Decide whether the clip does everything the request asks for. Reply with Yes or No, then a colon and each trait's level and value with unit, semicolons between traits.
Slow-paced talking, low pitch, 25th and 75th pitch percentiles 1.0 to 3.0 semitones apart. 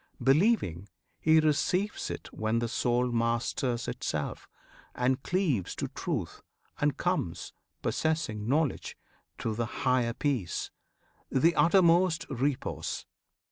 No: slow, 105 wpm; low, 130 Hz; average, 5.3 semitones